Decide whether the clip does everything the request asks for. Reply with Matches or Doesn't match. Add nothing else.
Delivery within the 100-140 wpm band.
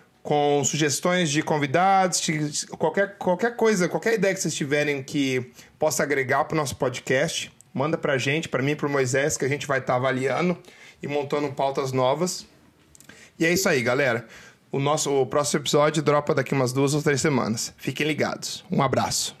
Doesn't match